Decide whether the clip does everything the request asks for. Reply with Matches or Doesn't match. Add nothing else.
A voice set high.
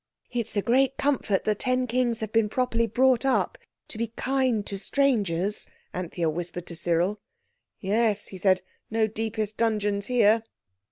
Matches